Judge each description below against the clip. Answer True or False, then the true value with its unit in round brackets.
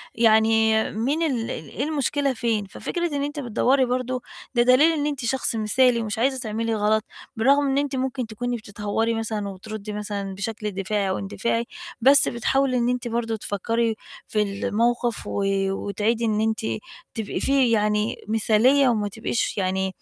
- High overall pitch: True (225 Hz)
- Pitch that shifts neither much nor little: True (3.2 semitones)